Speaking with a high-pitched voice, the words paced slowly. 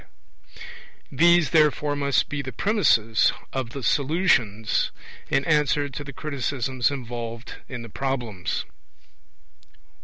No: low, 135 Hz; slow, 110 wpm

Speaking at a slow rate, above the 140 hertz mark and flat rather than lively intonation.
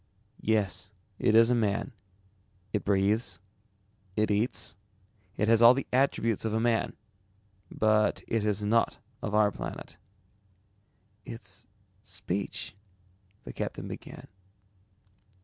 No: slow, 115 wpm; low, 105 Hz; narrow, 2.3 semitones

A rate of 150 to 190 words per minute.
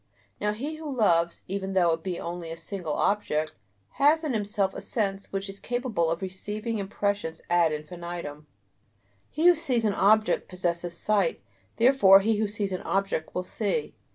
Yes: average, 170 wpm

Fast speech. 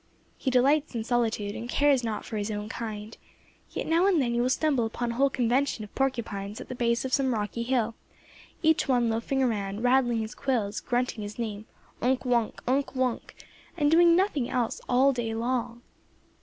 No: average, 190 wpm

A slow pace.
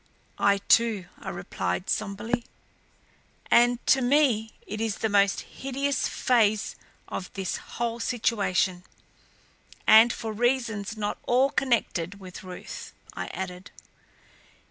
Yes: slow, 115 wpm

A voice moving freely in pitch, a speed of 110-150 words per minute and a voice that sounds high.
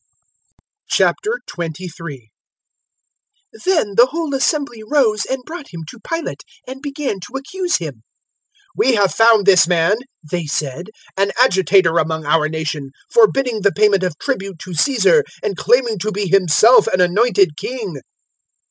Yes: wide, 7.3 semitones; average, 140 wpm; high, 205 Hz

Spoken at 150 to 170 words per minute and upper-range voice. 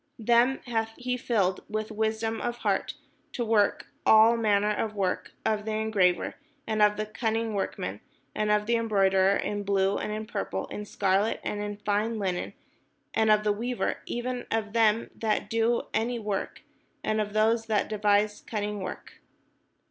Yes: average, 165 wpm; high, 215 Hz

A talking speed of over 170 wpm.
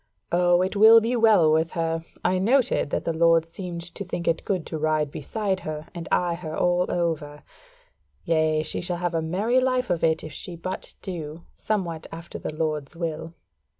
Yes: average, 190 wpm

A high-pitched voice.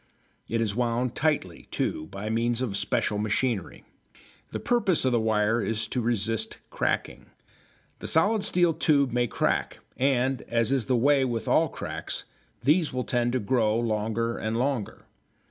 No: low, 120 Hz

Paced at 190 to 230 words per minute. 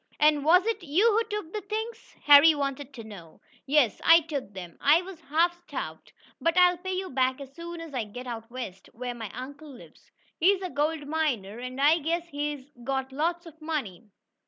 Yes: average, 200 wpm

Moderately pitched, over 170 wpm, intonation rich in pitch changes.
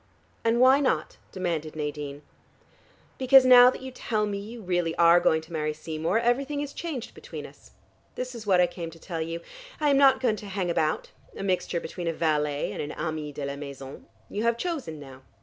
Yes: medium, 175 Hz; fast, 205 wpm; wide, 7.6 semitones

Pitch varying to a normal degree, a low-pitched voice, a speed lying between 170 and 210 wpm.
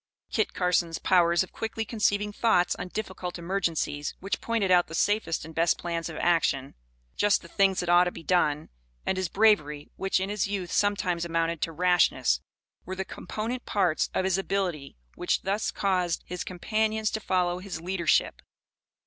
No: average, 3.0 semitones; medium, 180 Hz; average, 175 wpm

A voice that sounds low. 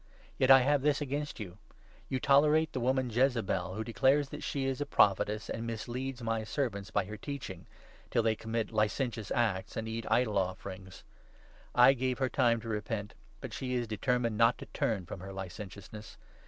Yes: low, 115 Hz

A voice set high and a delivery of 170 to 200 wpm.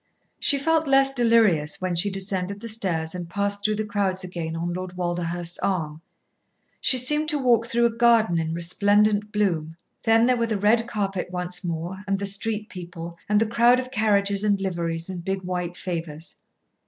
Yes: high, 195 Hz; average, 185 wpm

